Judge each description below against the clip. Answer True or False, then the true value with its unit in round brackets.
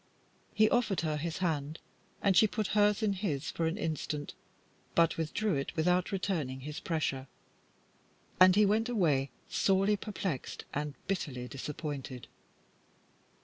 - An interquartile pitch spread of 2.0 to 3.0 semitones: False (5.3 semitones)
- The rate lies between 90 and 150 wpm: True (135 wpm)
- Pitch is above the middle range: False (170 Hz)